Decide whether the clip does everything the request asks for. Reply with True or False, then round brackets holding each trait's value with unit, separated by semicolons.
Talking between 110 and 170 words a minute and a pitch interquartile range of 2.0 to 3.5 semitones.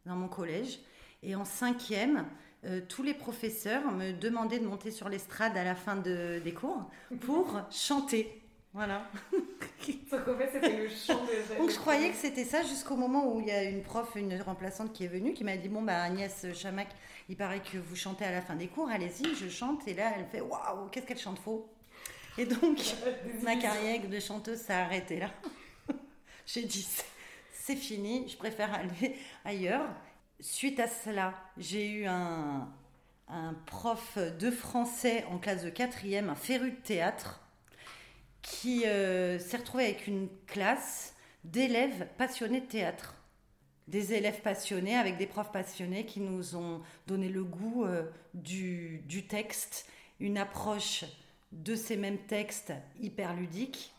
False (160 wpm; 4.5 semitones)